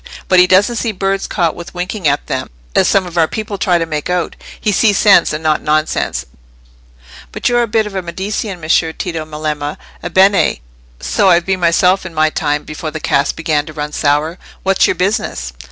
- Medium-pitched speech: Yes, medium, 175 Hz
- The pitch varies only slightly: No, average, 3.9 semitones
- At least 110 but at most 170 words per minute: No, average, 200 wpm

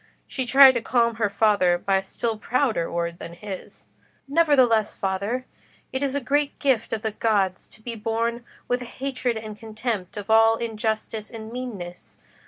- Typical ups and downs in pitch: Yes, average, 3.2 semitones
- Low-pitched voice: No, high, 225 Hz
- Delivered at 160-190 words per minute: Yes, average, 175 wpm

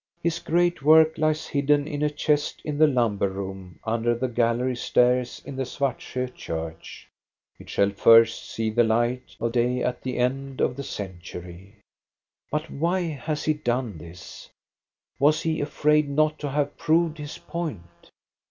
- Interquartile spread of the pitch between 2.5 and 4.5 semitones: No, average, 4.9 semitones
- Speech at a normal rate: Yes, average, 160 wpm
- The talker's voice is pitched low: Yes, low, 130 Hz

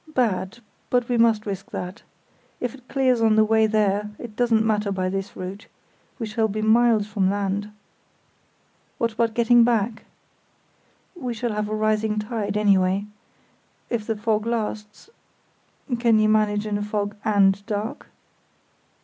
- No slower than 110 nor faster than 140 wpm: No, average, 150 wpm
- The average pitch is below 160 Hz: No, high, 215 Hz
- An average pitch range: No, narrow, 2.1 semitones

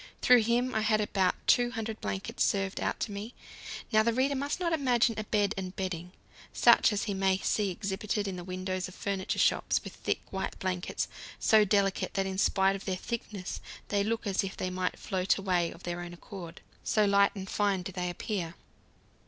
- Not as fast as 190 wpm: No, average, 200 wpm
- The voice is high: Yes, high, 195 Hz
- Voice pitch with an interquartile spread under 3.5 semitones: Yes, narrow, 2.6 semitones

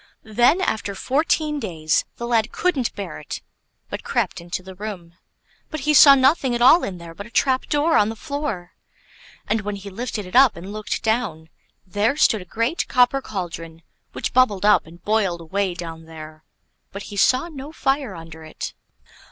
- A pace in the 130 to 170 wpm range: No, average, 185 wpm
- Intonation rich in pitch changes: Yes, wide, 6.7 semitones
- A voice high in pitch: Yes, high, 210 Hz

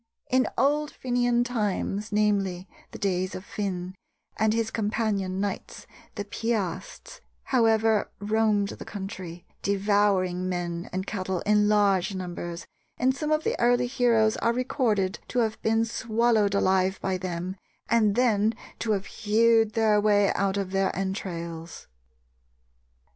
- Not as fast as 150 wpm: Yes, average, 140 wpm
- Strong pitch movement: No, average, 3.1 semitones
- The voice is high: Yes, high, 205 Hz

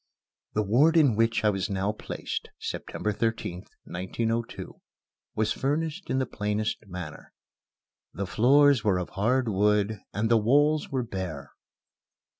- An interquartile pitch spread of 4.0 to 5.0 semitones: Yes, average, 4.6 semitones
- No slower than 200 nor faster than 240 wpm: No, slow, 135 wpm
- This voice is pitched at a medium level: No, low, 110 Hz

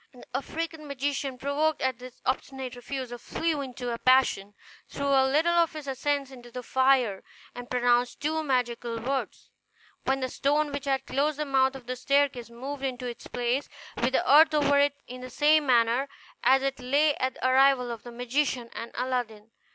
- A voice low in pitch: No, very high, 265 Hz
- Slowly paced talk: No, average, 185 wpm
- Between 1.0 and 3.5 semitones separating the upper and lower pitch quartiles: Yes, narrow, 2.5 semitones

